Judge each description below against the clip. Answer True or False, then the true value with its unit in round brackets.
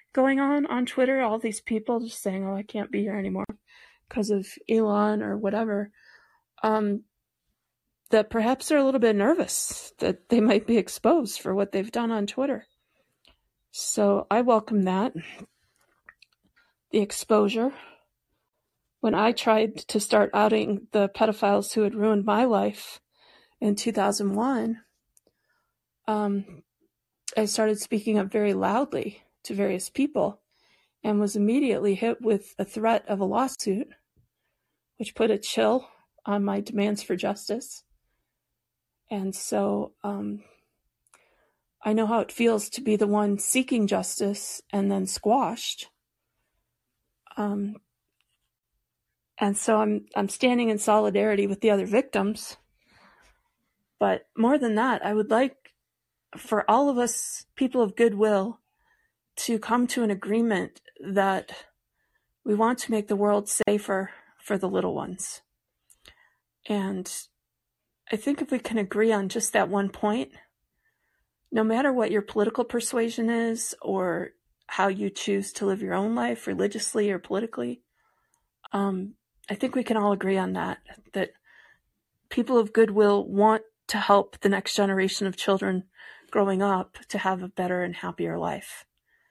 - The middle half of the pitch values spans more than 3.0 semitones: False (2.5 semitones)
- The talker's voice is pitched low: False (215 Hz)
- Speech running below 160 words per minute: True (140 wpm)